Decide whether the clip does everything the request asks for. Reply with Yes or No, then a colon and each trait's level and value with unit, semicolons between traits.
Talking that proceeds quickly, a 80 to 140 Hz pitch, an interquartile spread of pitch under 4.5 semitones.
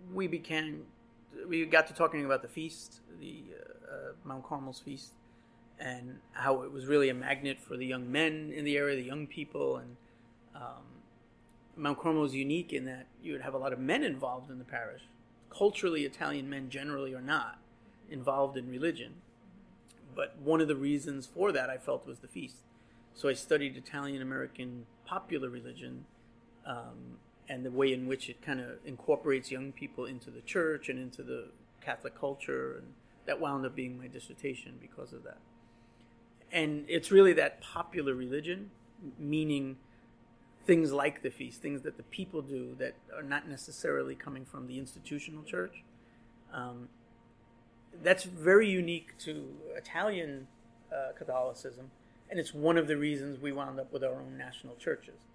No: average, 170 wpm; low, 135 Hz; average, 3.9 semitones